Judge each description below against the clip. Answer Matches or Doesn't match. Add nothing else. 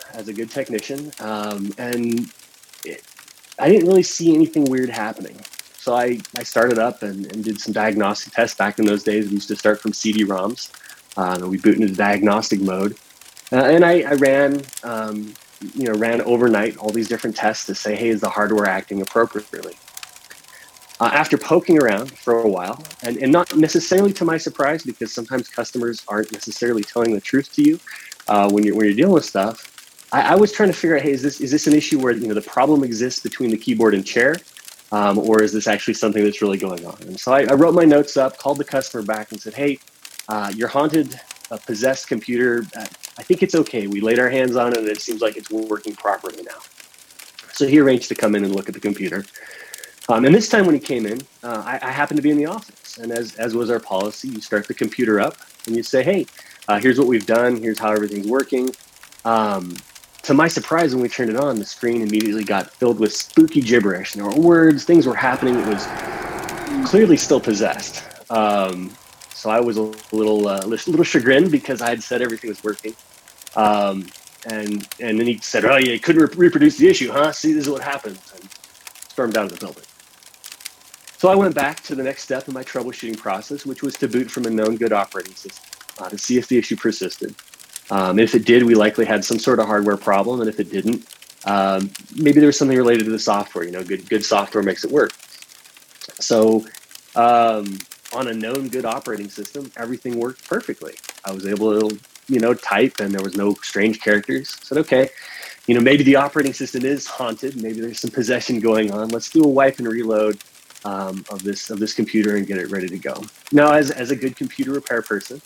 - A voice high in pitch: Doesn't match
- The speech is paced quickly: Matches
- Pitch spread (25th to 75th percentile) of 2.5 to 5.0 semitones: Matches